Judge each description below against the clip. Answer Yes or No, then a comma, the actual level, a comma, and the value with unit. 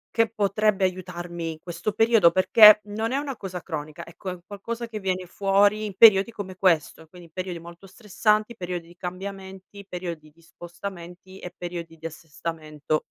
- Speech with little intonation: No, average, 3.1 semitones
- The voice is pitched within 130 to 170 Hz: No, medium, 185 Hz